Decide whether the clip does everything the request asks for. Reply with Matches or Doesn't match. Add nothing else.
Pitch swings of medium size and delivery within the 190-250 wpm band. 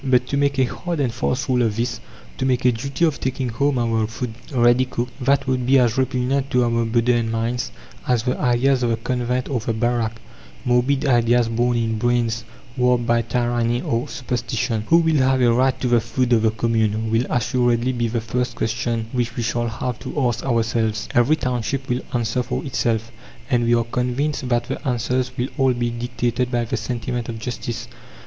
Doesn't match